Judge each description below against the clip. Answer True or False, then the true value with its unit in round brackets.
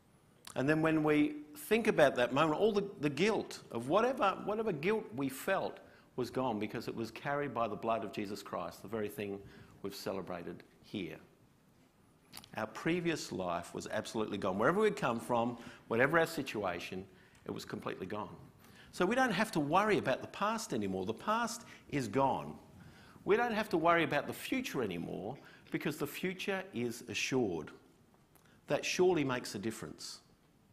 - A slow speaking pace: False (170 wpm)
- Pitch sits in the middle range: True (150 Hz)